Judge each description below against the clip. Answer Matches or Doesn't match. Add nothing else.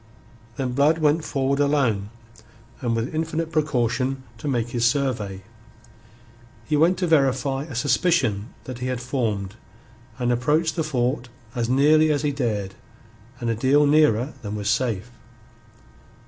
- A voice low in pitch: Matches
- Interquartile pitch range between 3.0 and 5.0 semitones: Matches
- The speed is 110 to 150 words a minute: Matches